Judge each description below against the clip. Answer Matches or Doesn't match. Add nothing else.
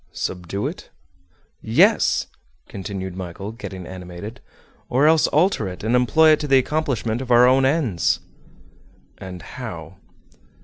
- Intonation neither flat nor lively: Doesn't match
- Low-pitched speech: Matches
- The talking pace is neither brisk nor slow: Doesn't match